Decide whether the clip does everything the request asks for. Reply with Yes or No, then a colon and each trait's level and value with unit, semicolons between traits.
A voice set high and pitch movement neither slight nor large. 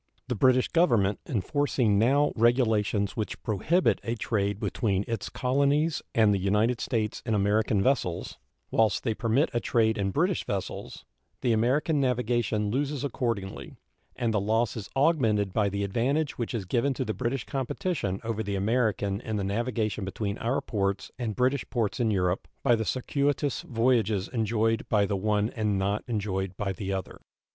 No: low, 110 Hz; average, 3.8 semitones